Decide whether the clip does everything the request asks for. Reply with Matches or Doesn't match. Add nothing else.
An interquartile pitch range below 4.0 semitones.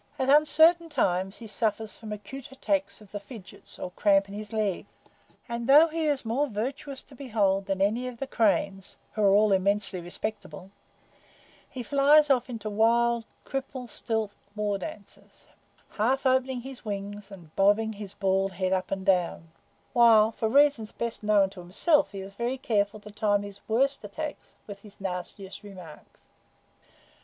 Doesn't match